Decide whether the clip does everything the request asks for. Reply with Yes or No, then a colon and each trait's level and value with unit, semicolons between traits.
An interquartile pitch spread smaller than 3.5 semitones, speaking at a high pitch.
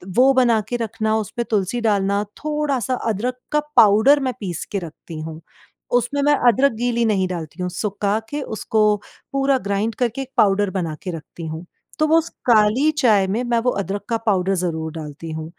No: average, 5.0 semitones; high, 215 Hz